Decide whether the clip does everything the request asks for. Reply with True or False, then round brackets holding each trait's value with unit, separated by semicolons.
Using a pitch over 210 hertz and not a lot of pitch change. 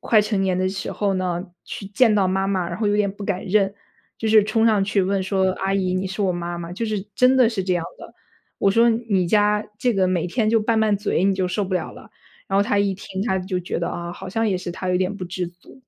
False (195 Hz; 2.3 semitones)